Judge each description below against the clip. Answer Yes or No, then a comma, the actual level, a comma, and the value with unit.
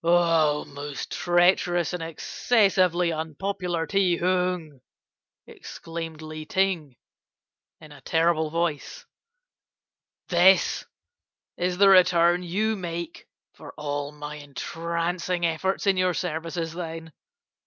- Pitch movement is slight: Yes, narrow, 2.3 semitones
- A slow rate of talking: Yes, slow, 100 wpm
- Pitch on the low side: No, medium, 170 Hz